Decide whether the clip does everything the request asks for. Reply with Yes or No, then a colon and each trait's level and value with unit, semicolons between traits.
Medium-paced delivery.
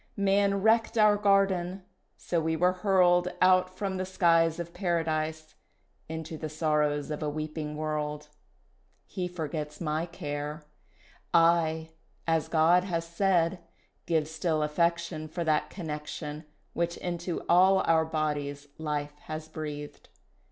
No: slow, 130 wpm